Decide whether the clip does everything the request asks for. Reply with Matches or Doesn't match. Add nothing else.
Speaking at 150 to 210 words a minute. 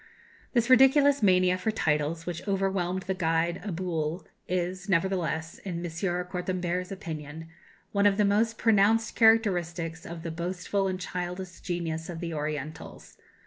Doesn't match